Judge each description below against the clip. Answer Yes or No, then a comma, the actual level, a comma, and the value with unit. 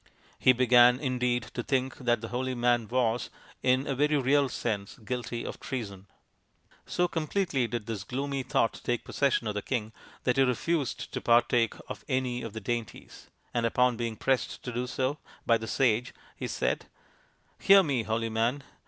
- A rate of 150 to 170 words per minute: No, average, 180 wpm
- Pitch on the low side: Yes, low, 125 Hz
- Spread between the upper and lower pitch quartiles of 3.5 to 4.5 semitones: No, narrow, 2.4 semitones